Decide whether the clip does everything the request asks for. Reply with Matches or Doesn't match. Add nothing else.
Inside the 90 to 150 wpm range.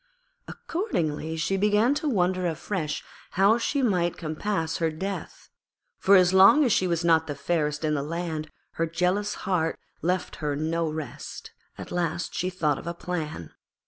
Doesn't match